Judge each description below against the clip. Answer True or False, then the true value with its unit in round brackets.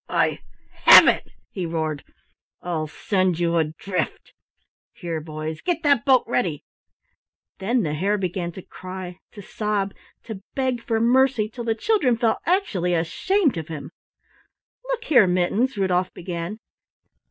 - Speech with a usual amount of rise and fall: False (5.9 semitones)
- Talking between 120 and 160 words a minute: True (140 wpm)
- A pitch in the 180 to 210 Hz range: True (190 Hz)